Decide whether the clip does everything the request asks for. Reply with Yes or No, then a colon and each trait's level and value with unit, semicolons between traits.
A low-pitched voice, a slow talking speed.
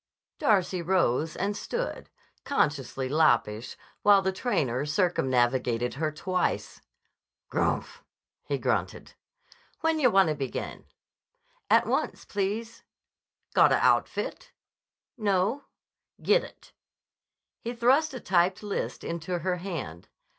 No: medium, 185 Hz; slow, 100 wpm